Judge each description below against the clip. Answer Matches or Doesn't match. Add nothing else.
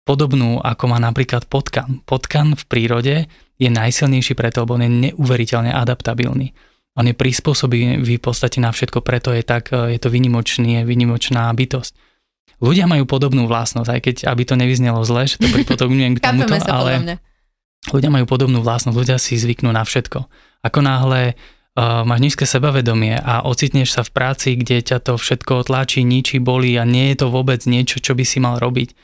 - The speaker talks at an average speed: Doesn't match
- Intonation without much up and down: Matches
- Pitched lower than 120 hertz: Doesn't match